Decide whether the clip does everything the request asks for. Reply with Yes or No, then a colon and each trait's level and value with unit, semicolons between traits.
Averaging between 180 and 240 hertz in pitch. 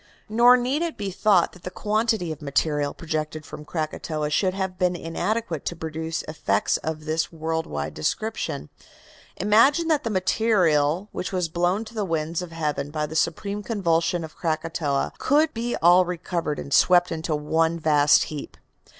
No: medium, 170 Hz